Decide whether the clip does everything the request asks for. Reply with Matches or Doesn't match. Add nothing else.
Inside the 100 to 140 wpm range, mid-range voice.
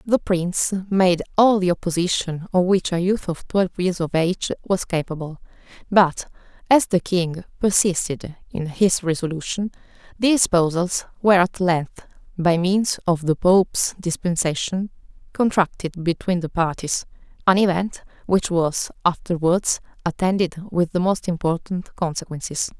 Matches